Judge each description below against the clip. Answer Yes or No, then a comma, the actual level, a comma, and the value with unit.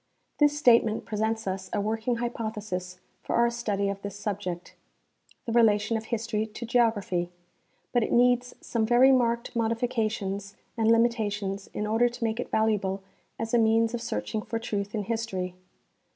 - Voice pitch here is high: Yes, high, 220 Hz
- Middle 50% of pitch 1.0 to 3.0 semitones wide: Yes, narrow, 2.5 semitones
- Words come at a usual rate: Yes, average, 170 wpm